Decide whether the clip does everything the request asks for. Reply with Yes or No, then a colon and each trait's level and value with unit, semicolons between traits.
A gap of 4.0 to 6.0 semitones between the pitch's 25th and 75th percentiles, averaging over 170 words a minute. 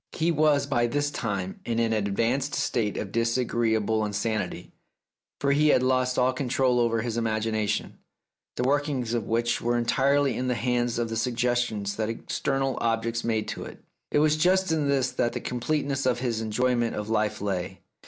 No: average, 3.1 semitones; average, 180 wpm